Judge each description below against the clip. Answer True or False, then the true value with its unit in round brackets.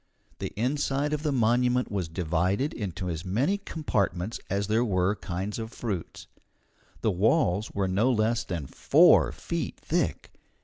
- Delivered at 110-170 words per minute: True (145 wpm)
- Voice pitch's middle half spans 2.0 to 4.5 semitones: False (5.0 semitones)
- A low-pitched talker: True (105 Hz)